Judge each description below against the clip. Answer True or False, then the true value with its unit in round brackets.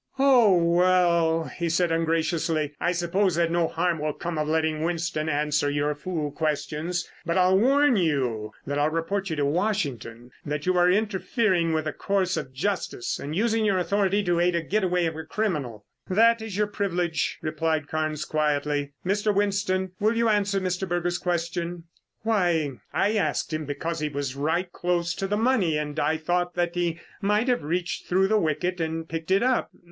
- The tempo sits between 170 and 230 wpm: True (180 wpm)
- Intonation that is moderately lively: True (3.6 semitones)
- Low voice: False (170 Hz)